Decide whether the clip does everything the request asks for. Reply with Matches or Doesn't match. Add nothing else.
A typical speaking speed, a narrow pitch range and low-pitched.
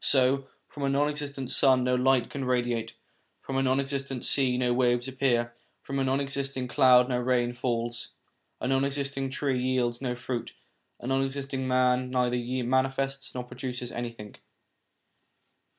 Matches